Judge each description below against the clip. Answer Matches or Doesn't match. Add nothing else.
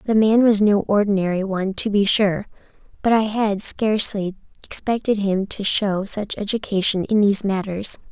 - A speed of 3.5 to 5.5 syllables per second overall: Matches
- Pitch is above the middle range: Matches